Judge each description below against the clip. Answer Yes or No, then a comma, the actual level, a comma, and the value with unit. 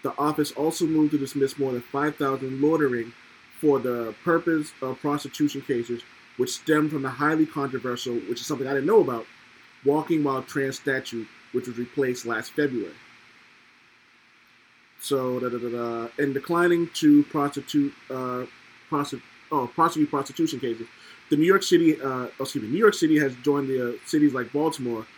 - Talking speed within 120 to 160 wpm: Yes, average, 155 wpm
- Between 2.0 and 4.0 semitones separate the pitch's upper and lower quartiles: Yes, average, 3.3 semitones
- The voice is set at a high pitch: No, medium, 140 Hz